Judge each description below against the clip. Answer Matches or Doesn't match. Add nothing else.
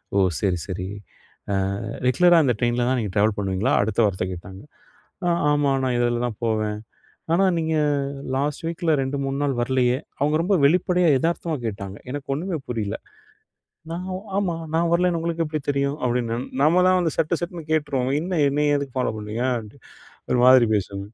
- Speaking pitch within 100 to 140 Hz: Matches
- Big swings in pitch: Matches